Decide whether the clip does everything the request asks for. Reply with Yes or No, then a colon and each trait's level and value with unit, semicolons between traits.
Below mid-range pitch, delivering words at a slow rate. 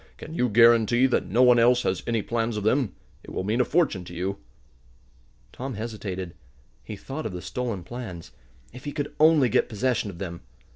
No: low, 115 Hz; average, 195 wpm